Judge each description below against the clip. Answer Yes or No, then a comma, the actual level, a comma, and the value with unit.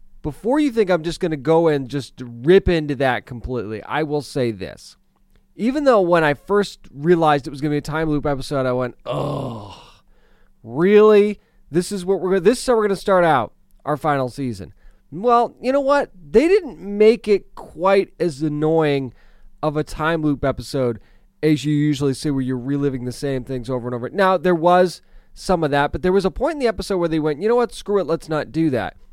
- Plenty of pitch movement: Yes, wide, 5.9 semitones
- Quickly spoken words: Yes, fast, 220 wpm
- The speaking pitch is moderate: Yes, medium, 155 Hz